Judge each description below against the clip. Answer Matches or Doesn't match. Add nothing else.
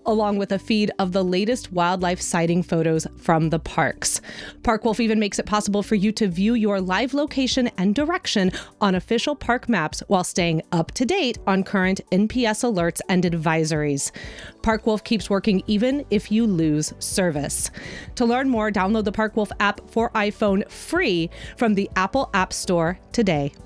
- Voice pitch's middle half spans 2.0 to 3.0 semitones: Doesn't match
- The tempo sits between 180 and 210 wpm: Doesn't match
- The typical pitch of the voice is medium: Doesn't match